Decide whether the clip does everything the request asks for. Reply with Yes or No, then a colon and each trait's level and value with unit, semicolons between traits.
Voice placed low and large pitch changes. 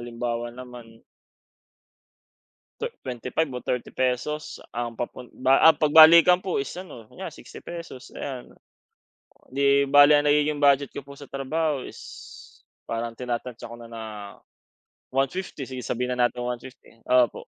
No: low, 130 Hz; average, 3.2 semitones